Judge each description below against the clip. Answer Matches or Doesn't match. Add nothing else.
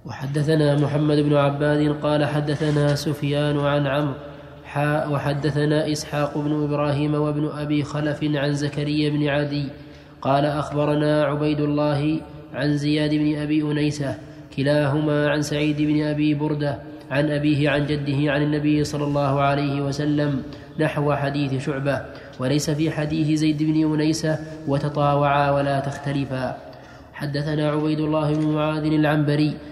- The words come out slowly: Doesn't match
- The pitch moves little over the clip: Matches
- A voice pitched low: Doesn't match